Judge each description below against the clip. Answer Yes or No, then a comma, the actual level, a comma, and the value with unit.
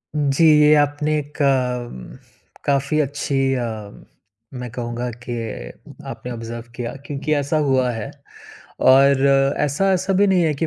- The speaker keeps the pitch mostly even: No, average, 3.3 semitones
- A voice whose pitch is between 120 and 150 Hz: Yes, medium, 140 Hz